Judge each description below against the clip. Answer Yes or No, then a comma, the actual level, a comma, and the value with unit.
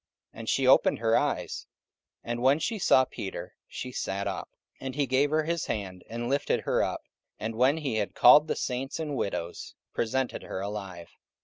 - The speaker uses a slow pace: No, average, 190 wpm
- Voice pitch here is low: Yes, low, 125 Hz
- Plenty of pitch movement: No, average, 4.8 semitones